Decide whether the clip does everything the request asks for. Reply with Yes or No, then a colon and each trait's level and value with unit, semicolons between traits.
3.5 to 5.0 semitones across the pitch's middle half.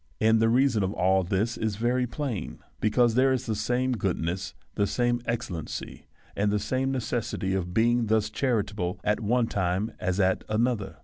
Yes: average, 4.0 semitones